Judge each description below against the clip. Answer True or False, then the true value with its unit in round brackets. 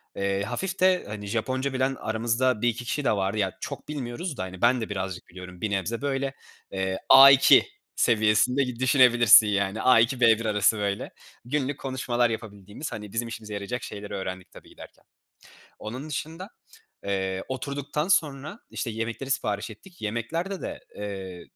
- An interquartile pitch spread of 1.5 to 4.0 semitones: False (4.7 semitones)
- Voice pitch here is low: True (115 Hz)